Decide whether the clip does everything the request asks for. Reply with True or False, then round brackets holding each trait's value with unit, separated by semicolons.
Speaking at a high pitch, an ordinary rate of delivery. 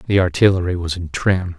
False (90 Hz; 190 wpm)